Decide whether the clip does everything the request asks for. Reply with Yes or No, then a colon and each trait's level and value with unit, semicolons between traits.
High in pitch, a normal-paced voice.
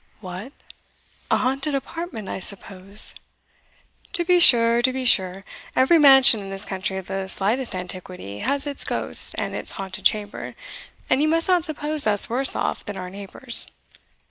Yes: high, 230 Hz; average, 165 wpm